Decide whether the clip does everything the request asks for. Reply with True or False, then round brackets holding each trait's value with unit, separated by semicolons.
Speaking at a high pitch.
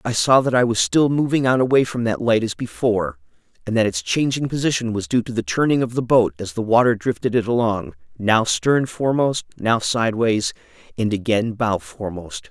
False (115 Hz)